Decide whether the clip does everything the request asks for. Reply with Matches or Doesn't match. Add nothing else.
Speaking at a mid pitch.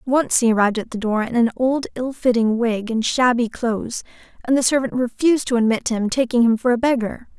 Doesn't match